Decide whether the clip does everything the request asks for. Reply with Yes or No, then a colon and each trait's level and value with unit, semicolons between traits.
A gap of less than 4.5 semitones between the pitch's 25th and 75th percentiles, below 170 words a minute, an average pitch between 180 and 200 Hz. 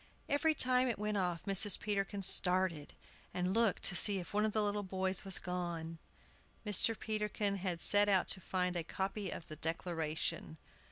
No: average, 2.8 semitones; average, 175 wpm; high, 190 Hz